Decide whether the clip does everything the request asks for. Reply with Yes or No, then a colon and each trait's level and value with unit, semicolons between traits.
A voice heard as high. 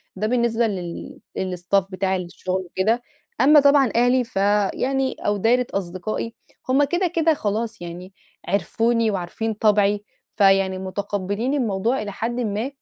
Yes: high, 215 Hz